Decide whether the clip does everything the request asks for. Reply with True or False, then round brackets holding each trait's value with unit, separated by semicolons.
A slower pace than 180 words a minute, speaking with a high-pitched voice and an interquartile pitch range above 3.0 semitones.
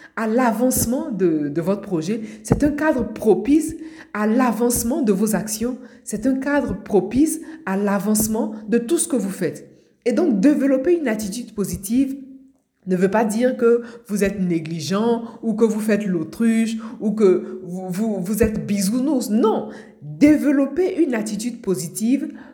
True (155 wpm; 230 Hz; 4.4 semitones)